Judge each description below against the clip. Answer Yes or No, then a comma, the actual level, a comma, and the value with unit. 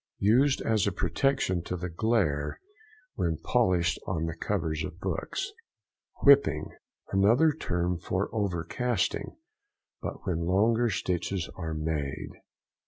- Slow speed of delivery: Yes, slow, 110 wpm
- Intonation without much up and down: No, average, 5.1 semitones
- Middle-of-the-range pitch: No, very low, 90 Hz